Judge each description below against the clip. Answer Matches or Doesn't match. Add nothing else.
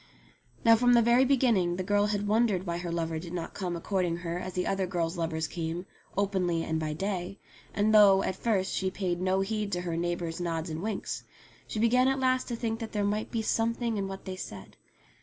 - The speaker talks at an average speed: Doesn't match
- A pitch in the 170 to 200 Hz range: Matches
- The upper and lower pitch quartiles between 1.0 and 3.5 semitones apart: Doesn't match